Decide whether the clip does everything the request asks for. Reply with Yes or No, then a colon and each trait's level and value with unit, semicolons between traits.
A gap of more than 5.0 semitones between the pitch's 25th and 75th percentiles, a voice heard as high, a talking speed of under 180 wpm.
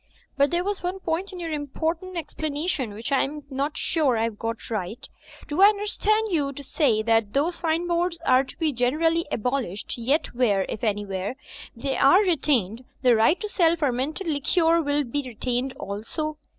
No: wide, 5.6 semitones; very high, 285 Hz; average, 185 wpm